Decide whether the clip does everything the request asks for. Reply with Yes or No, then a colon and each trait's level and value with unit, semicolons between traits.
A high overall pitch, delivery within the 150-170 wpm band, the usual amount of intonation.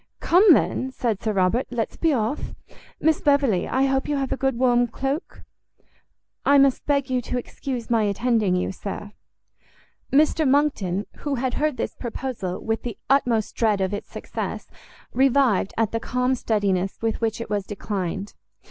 Yes: high, 240 Hz; average, 165 wpm; average, 4.5 semitones